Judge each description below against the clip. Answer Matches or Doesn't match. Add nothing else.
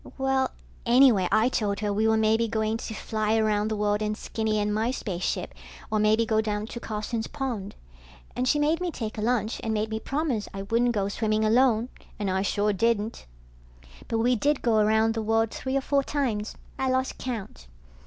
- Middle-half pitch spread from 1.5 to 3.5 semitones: Matches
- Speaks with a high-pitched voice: Matches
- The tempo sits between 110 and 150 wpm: Doesn't match